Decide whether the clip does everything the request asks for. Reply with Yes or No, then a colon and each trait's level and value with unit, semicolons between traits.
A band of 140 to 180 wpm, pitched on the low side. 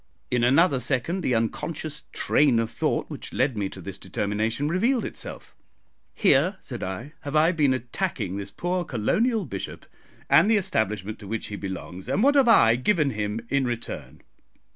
Yes: average, 170 wpm; low, 130 Hz